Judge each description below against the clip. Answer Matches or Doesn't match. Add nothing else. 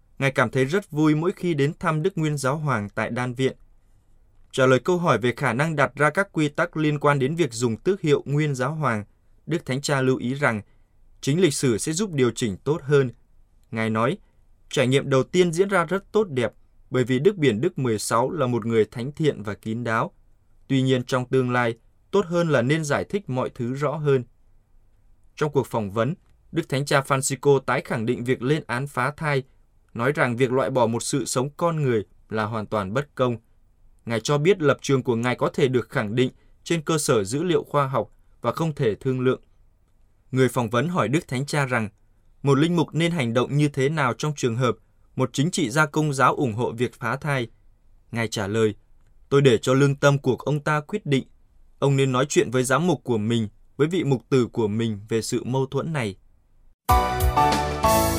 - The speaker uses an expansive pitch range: Doesn't match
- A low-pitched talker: Matches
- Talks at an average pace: Matches